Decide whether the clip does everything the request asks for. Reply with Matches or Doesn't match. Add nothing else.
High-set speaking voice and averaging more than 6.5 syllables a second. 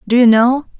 Doesn't match